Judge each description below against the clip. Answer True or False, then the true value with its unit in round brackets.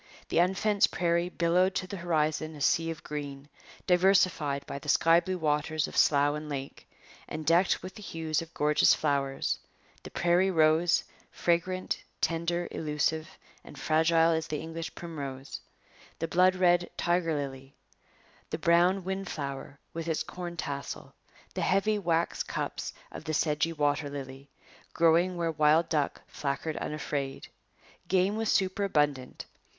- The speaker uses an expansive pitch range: False (2.9 semitones)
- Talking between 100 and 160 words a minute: True (145 wpm)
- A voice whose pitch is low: False (165 Hz)